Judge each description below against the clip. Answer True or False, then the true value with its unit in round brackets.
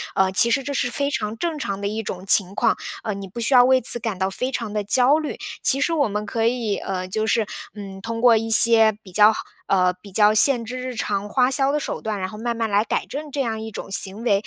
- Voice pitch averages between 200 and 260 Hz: True (220 Hz)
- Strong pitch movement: False (3.7 semitones)